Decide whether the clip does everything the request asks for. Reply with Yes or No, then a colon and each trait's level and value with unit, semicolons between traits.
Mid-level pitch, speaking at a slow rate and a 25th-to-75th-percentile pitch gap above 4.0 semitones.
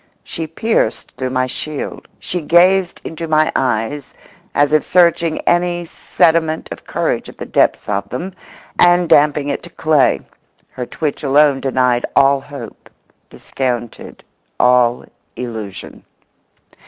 Yes: medium, 145 Hz; slow, 130 wpm; average, 4.6 semitones